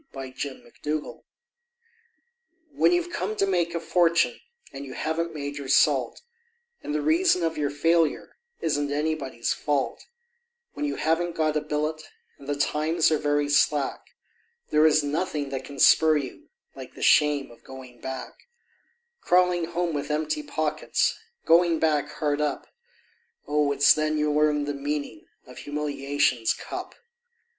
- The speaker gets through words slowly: No, average, 155 wpm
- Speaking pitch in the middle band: Yes, medium, 150 Hz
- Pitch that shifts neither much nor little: No, narrow, 2.0 semitones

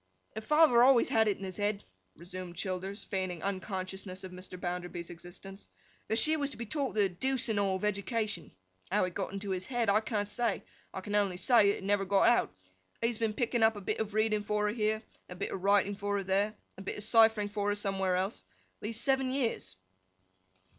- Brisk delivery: Yes, fast, 215 wpm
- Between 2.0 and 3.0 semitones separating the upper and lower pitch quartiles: Yes, average, 2.7 semitones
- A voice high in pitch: Yes, high, 205 Hz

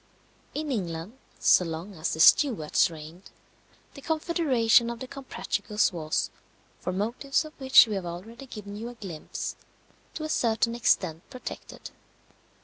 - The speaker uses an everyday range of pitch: No, wide, 7.0 semitones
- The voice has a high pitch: Yes, high, 225 Hz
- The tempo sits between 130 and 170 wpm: Yes, average, 145 wpm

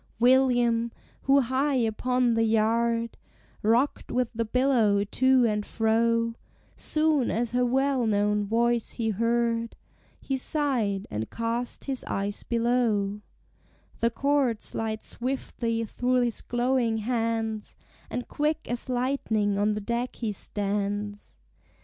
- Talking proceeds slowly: Yes, slow, 125 wpm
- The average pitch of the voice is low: No, high, 230 Hz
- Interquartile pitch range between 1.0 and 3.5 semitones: Yes, narrow, 2.5 semitones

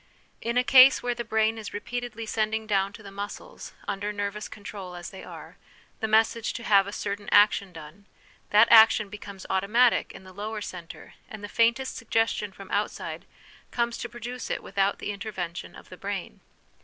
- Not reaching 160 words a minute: No, average, 180 wpm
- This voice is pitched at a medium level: No, high, 210 Hz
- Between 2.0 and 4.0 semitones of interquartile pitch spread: Yes, narrow, 2.5 semitones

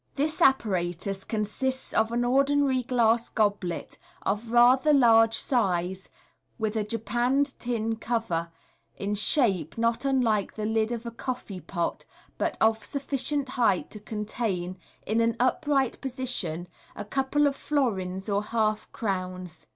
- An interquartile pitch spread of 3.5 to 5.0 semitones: Yes, average, 4.2 semitones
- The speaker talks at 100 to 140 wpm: Yes, slow, 135 wpm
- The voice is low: No, high, 225 Hz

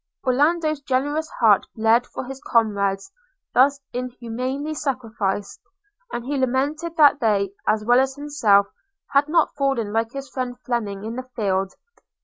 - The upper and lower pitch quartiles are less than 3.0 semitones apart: No, average, 4.2 semitones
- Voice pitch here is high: Yes, very high, 255 Hz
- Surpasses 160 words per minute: No, average, 140 wpm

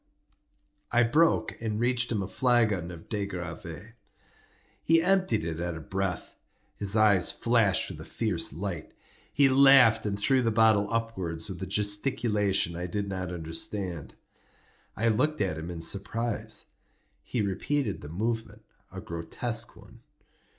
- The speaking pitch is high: No, low, 105 Hz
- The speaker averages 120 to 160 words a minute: Yes, average, 145 wpm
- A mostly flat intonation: No, average, 4.7 semitones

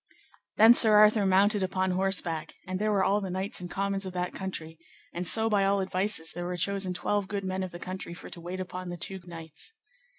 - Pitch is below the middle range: No, high, 190 Hz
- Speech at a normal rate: No, fast, 225 wpm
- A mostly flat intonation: Yes, narrow, 1.9 semitones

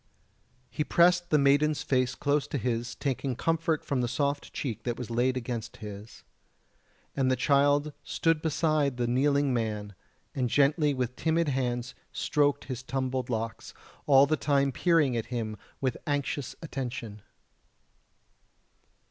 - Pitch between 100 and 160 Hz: Yes, low, 135 Hz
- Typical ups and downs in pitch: Yes, average, 3.0 semitones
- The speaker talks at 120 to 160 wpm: Yes, average, 140 wpm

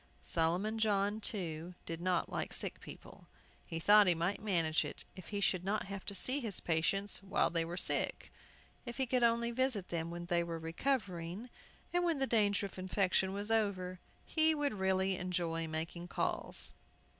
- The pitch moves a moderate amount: Yes, average, 4.0 semitones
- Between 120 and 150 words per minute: No, average, 180 wpm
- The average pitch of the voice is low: No, high, 190 Hz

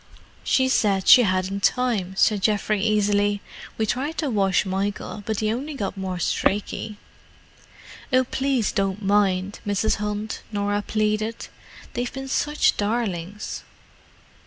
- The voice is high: Yes, high, 210 Hz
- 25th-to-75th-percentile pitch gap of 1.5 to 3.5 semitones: Yes, narrow, 2.6 semitones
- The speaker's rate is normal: No, slow, 130 wpm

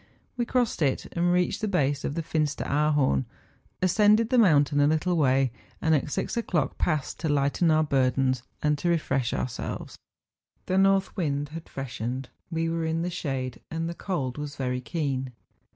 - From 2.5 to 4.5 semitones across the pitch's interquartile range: Yes, average, 4.2 semitones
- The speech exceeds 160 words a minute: Yes, average, 180 wpm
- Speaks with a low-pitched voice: No, medium, 150 Hz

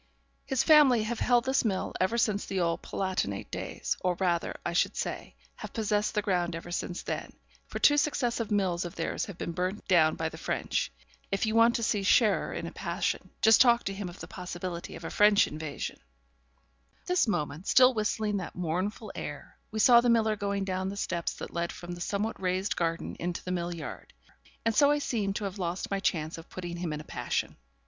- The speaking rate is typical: No, fast, 215 wpm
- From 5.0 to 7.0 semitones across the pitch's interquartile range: No, average, 4.1 semitones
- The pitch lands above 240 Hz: No, high, 195 Hz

